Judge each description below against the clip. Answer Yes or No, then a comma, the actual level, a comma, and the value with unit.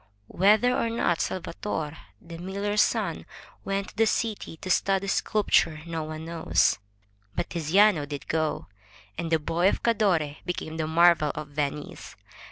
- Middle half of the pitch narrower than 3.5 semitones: No, average, 4.1 semitones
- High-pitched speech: No, medium, 170 Hz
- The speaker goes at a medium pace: Yes, average, 150 wpm